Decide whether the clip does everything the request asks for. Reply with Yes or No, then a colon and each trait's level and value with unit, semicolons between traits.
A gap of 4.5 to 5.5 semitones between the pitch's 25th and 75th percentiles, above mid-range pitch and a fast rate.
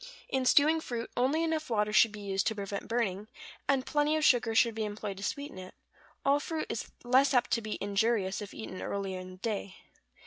Yes: average, 5.2 semitones; high, 225 Hz; fast, 210 wpm